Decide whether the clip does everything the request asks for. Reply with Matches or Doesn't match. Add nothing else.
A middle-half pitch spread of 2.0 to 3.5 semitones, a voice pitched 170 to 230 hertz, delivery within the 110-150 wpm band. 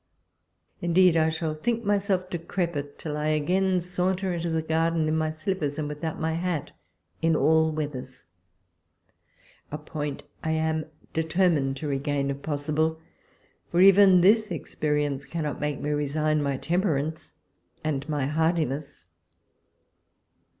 Doesn't match